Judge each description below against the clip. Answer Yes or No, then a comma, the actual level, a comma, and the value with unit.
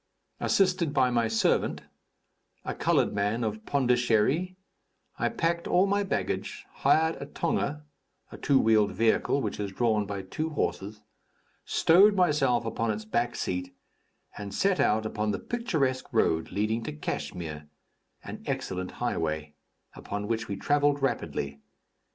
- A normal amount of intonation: No, wide, 6.4 semitones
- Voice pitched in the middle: No, low, 115 Hz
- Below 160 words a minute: Yes, average, 140 wpm